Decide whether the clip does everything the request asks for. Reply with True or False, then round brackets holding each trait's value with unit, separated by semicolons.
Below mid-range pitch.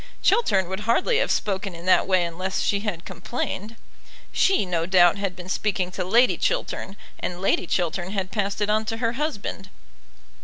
False (195 Hz)